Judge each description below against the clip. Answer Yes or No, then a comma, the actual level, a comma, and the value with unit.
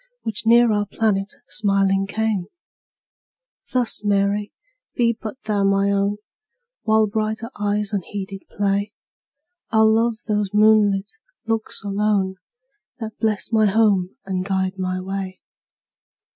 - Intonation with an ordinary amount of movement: No, narrow, 1.9 semitones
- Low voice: No, high, 205 Hz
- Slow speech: Yes, slow, 115 wpm